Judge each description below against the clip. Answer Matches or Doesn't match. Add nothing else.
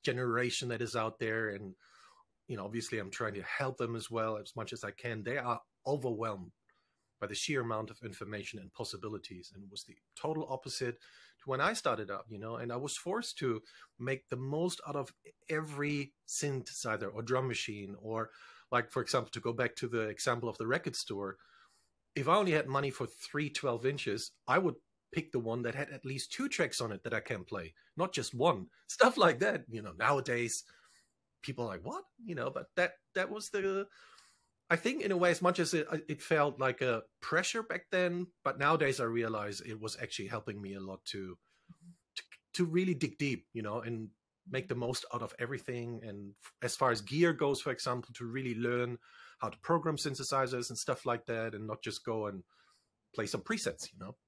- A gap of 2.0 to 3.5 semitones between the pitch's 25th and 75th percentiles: Doesn't match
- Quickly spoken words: Matches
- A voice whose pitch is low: Matches